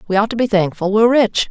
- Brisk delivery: Yes, fast, 280 wpm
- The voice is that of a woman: Yes, female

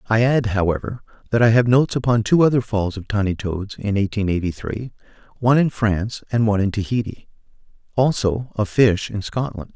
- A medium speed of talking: Yes, average, 185 wpm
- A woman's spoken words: No, male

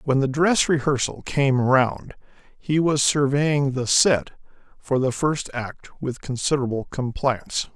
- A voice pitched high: No, low, 135 Hz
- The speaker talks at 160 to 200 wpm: No, average, 140 wpm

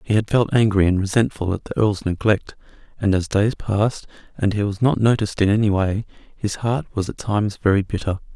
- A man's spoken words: Yes, male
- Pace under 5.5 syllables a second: No, 5.7 syllables/s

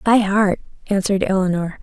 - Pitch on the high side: Yes, high, 195 Hz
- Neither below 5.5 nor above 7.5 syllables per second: Yes, 5.6 syllables/s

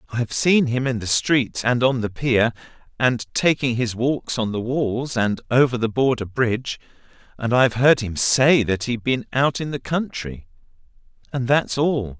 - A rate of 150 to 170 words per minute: No, average, 180 wpm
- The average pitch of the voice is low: Yes, low, 125 Hz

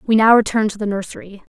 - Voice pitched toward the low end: No, high, 210 Hz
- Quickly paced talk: Yes, fast, 235 wpm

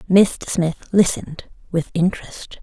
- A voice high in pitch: No, medium, 180 Hz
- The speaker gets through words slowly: Yes, slow, 115 wpm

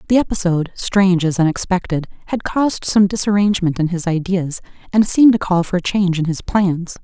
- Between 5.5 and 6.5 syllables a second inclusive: Yes, 5.9 syllables/s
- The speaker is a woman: Yes, female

